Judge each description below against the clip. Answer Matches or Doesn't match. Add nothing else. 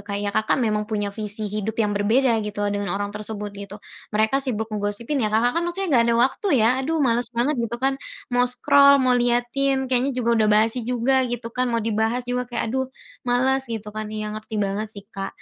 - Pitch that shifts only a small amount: Doesn't match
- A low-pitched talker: Doesn't match